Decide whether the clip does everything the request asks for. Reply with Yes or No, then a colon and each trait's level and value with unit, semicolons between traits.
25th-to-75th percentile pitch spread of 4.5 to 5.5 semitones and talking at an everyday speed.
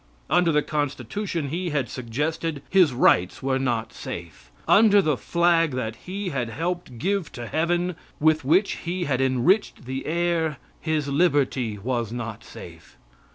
Yes: average, 5.2 semitones; average, 150 wpm